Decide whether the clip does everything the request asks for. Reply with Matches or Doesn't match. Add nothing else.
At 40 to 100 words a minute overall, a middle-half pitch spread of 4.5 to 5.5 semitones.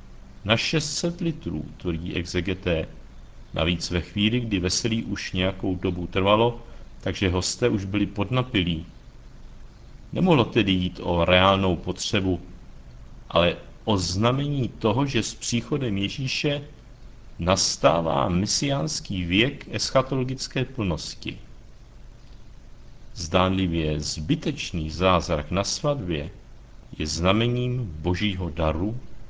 Matches